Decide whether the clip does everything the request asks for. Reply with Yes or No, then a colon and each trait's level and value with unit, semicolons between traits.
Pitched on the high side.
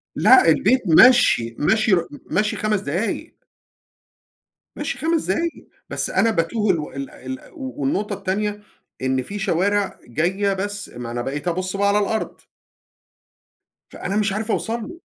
Yes: high, 200 Hz